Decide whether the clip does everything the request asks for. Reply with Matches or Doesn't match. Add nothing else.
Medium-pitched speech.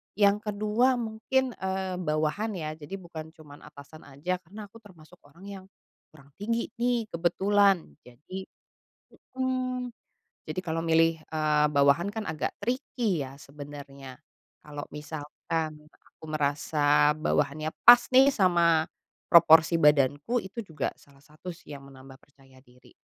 Matches